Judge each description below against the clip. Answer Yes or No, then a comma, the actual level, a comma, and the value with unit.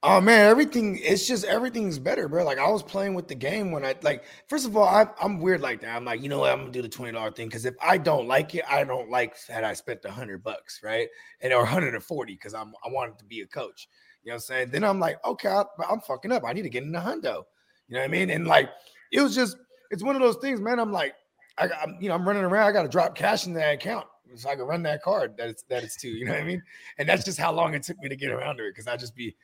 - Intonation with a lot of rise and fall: Yes, wide, 8.6 semitones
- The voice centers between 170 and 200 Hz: Yes, medium, 185 Hz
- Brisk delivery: Yes, fast, 305 wpm